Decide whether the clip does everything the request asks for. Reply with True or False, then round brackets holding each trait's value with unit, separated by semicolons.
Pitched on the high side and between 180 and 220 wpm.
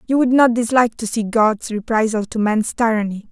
True (225 Hz; 200 wpm)